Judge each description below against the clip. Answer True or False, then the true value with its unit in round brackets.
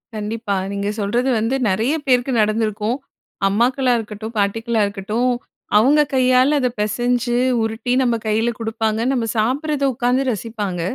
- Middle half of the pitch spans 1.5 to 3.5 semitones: True (2.9 semitones)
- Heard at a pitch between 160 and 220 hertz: False (230 Hz)